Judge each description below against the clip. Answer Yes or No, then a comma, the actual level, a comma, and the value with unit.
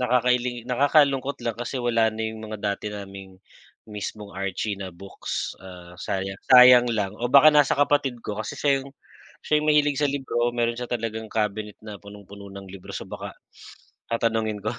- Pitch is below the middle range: Yes, low, 110 Hz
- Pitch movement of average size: Yes, average, 3.7 semitones